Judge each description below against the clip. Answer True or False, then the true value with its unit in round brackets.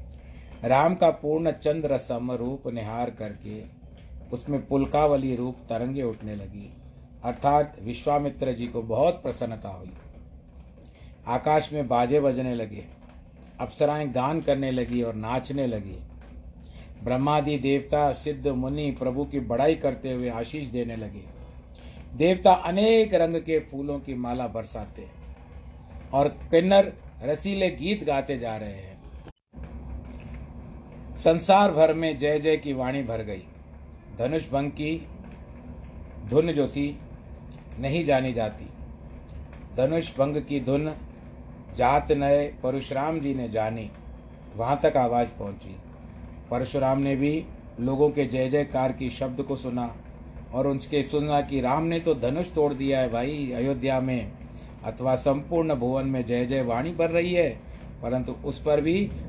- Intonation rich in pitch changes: True (6.5 semitones)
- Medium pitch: False (125 Hz)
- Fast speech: False (135 wpm)